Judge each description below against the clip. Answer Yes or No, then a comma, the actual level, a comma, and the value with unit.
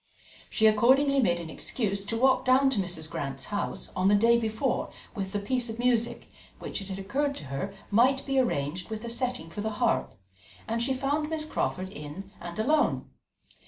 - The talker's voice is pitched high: Yes, high, 220 Hz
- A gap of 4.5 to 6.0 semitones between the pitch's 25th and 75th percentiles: Yes, average, 5.2 semitones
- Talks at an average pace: Yes, average, 195 wpm